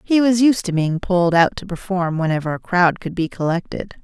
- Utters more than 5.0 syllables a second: Yes, 5.4 syllables/s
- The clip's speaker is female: Yes, female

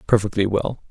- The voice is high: No, low, 105 Hz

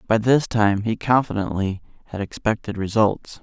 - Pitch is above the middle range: No, low, 110 Hz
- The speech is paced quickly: No, average, 140 wpm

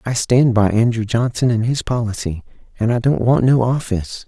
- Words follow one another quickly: No, average, 195 wpm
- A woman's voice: No, male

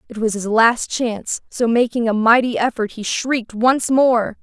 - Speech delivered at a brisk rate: No, average, 190 wpm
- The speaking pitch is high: Yes, high, 230 Hz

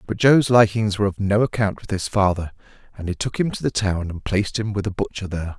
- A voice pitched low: Yes, low, 100 Hz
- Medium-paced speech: No, fast, 260 wpm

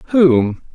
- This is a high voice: No, medium, 145 Hz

